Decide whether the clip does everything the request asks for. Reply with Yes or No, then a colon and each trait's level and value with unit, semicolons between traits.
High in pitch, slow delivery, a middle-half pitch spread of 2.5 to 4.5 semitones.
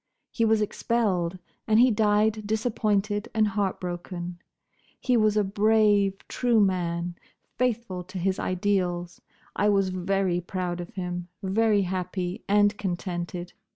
Yes: high, 195 Hz; slow, 125 wpm; average, 3.1 semitones